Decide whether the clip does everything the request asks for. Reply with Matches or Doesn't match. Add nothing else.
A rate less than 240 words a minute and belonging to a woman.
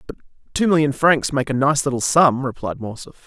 Doesn't match